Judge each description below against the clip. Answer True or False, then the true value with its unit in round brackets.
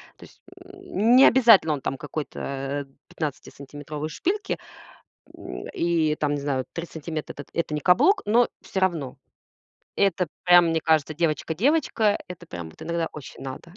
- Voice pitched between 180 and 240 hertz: False (160 Hz)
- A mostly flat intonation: False (4.5 semitones)